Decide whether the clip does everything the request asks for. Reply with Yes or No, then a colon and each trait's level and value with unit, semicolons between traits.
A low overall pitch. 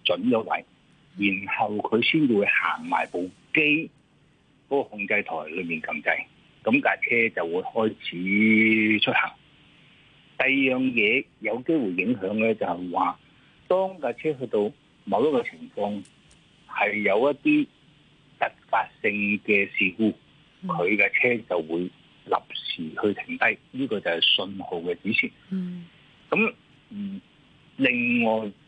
Yes: low, 130 Hz